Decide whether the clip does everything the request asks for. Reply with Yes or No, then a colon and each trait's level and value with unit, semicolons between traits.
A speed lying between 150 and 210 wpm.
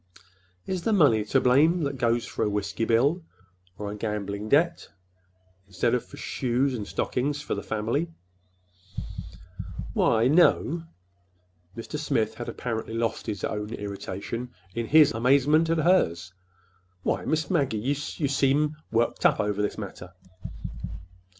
No: average, 140 wpm